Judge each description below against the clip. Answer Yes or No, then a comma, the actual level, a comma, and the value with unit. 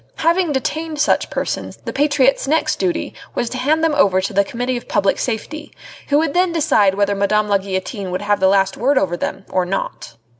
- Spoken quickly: Yes, fast, 210 wpm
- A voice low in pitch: No, high, 240 Hz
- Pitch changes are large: Yes, wide, 7.4 semitones